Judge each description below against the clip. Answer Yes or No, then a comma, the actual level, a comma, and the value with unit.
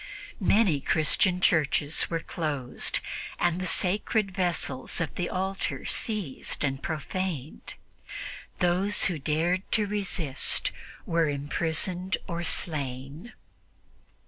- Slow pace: Yes, slow, 95 wpm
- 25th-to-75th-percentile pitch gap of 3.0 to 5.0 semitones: Yes, average, 3.9 semitones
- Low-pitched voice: No, medium, 170 Hz